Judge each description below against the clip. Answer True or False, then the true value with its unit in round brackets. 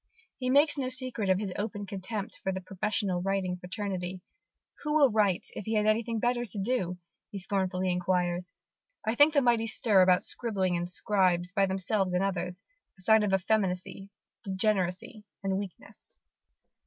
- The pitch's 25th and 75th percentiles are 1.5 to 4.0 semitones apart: True (3.1 semitones)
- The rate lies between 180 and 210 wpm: False (165 wpm)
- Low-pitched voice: False (195 Hz)